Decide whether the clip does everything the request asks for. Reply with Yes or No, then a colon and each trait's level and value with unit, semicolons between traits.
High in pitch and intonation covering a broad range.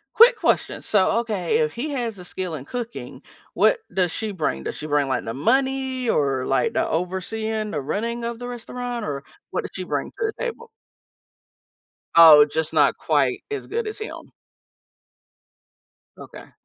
Yes: high, 215 Hz; wide, 8.3 semitones